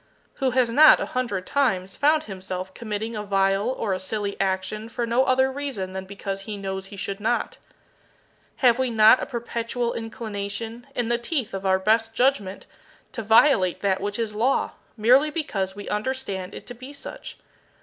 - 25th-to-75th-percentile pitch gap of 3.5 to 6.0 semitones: Yes, average, 4.1 semitones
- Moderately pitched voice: No, high, 220 Hz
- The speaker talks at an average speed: Yes, average, 180 wpm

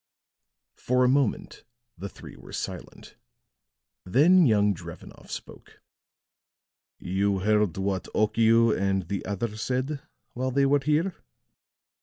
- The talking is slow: Yes, slow, 115 wpm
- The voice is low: Yes, low, 110 Hz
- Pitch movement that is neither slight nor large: Yes, average, 5.0 semitones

